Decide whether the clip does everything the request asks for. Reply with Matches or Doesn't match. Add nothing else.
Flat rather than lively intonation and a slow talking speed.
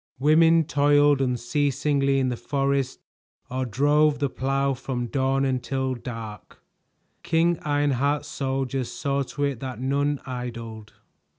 Matches